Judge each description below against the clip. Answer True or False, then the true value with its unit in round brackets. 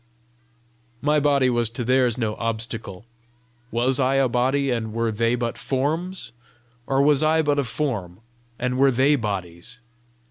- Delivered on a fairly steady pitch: False (3.3 semitones)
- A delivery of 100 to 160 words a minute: True (150 wpm)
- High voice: False (125 Hz)